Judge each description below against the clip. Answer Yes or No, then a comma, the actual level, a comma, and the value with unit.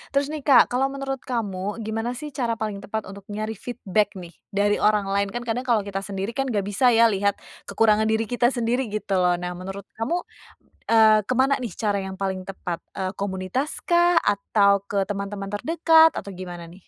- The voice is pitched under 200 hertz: No, high, 210 Hz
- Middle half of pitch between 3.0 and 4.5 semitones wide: Yes, average, 3.7 semitones